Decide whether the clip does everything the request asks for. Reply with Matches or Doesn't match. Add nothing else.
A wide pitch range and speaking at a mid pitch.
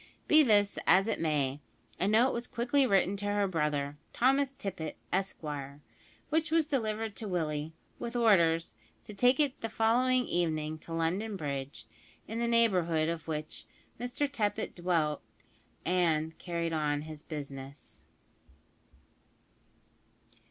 Matches